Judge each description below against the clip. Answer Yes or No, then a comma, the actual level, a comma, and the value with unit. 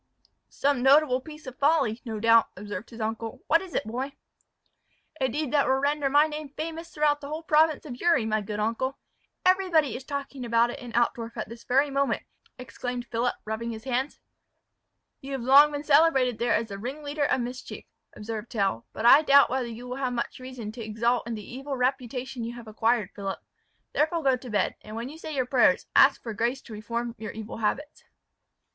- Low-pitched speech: No, very high, 250 Hz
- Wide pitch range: No, average, 3.9 semitones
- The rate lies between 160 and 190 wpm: No, average, 200 wpm